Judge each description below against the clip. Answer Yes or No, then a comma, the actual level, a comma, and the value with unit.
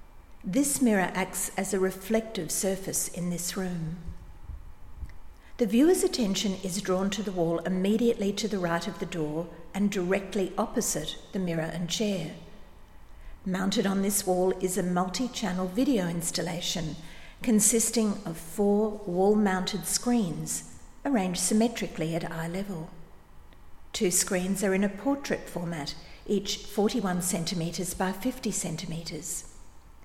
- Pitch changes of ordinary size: Yes, average, 3.7 semitones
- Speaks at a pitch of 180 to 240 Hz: Yes, high, 190 Hz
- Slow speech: Yes, slow, 130 wpm